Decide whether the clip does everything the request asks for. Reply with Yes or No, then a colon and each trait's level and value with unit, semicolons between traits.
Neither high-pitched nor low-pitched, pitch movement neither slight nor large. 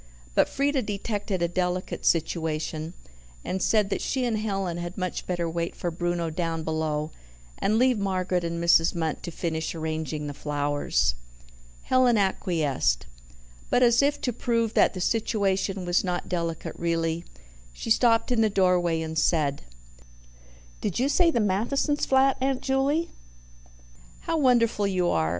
No: medium, 180 Hz; wide, 5.7 semitones